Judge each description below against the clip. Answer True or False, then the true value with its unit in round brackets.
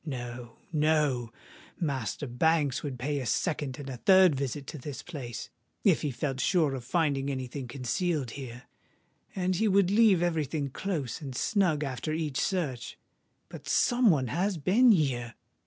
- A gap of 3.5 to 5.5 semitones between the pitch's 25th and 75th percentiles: True (5.0 semitones)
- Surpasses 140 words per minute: True (160 wpm)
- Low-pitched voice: False (145 Hz)